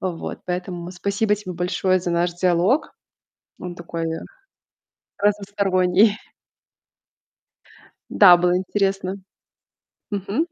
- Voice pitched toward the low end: No, medium, 185 Hz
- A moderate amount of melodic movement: No, narrow, 2.2 semitones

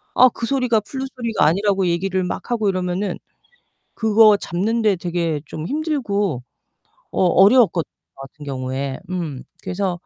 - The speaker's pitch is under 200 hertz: Yes, high, 190 Hz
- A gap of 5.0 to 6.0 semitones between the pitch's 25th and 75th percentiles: No, average, 4.6 semitones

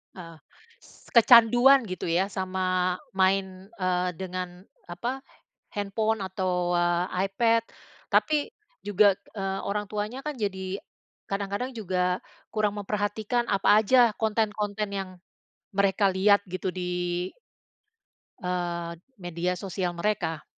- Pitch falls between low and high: No, high, 195 Hz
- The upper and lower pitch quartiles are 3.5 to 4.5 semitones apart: No, average, 2.7 semitones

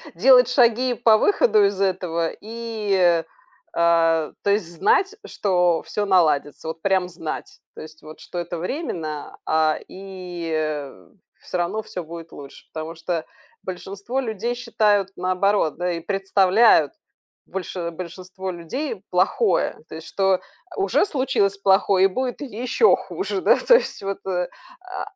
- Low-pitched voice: No, high, 190 Hz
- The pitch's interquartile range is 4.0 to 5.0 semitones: Yes, average, 4.7 semitones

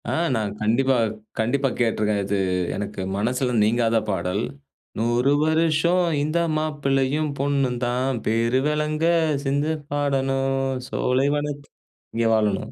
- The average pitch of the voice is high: No, low, 135 Hz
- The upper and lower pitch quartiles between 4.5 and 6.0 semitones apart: No, average, 4.0 semitones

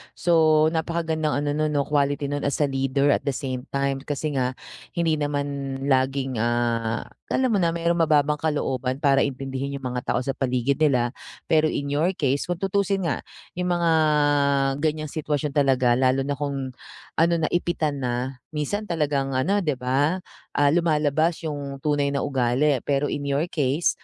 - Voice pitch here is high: No, medium, 145 Hz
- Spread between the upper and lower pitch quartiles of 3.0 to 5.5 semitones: No, narrow, 2.6 semitones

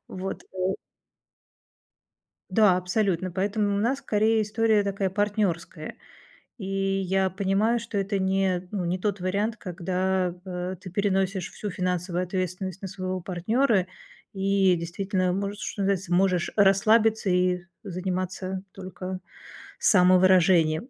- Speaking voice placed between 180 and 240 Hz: Yes, high, 190 Hz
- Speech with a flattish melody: Yes, narrow, 1.8 semitones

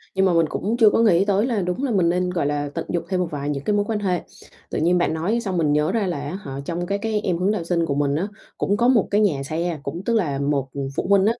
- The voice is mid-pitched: Yes, medium, 180 Hz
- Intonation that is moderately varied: Yes, average, 5.0 semitones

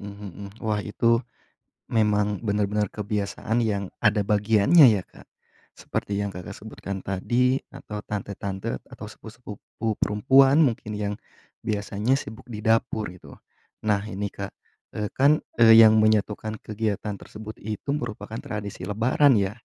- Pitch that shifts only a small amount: Yes, narrow, 1.7 semitones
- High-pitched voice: No, low, 105 Hz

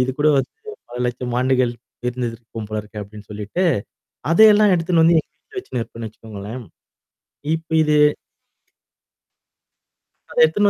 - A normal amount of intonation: No, wide, 6.9 semitones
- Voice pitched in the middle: No, low, 125 Hz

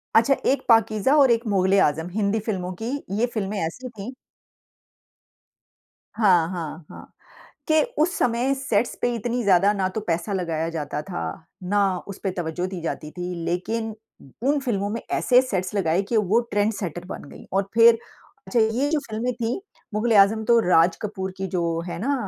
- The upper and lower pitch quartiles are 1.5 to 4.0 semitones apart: No, average, 4.4 semitones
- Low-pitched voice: No, high, 205 Hz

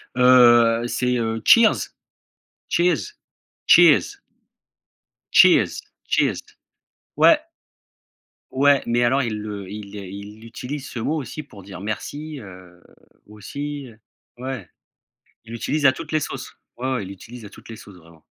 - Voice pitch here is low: Yes, low, 115 Hz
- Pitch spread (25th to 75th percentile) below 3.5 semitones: No, average, 4.5 semitones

